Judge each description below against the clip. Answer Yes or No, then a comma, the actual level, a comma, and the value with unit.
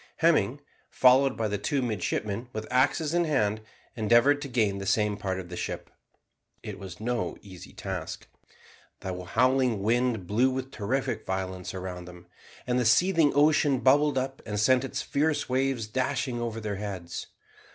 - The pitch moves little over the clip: No, average, 4.8 semitones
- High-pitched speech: No, low, 120 Hz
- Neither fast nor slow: Yes, average, 160 wpm